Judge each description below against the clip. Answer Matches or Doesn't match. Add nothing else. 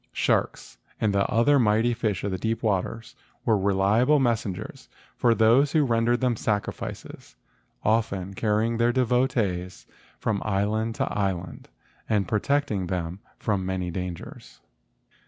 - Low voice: Matches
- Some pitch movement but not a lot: Matches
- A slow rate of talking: Matches